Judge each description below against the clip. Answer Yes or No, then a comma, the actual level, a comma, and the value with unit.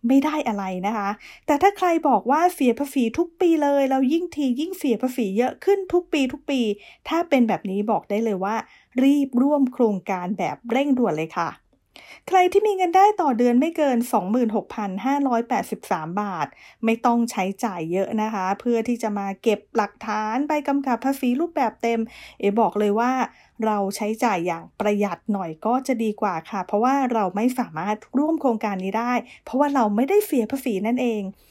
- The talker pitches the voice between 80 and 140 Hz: No, high, 240 Hz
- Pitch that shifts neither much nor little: Yes, average, 4.8 semitones